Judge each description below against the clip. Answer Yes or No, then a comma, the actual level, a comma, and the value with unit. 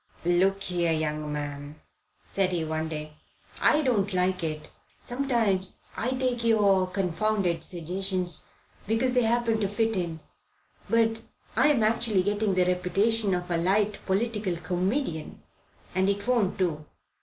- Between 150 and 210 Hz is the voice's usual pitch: Yes, high, 190 Hz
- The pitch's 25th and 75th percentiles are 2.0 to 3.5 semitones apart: No, average, 4.2 semitones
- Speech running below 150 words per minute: Yes, slow, 135 wpm